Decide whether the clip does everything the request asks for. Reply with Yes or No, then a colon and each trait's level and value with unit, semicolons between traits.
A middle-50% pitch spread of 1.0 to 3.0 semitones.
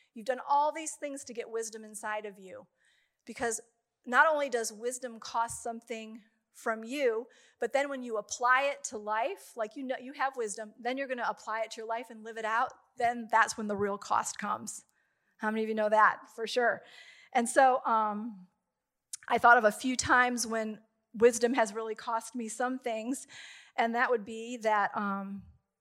Yes: narrow, 2.6 semitones